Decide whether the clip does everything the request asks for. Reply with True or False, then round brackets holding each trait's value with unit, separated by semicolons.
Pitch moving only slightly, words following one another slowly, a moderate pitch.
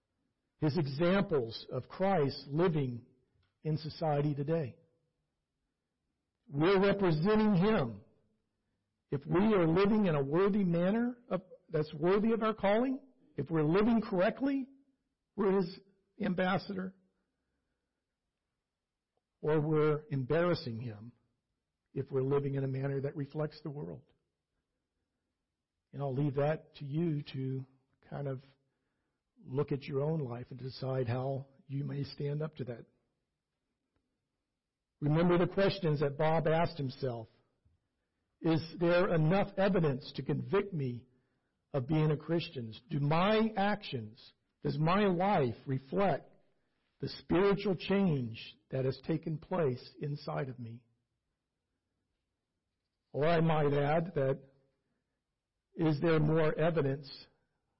False (5.2 semitones; 115 wpm; 150 Hz)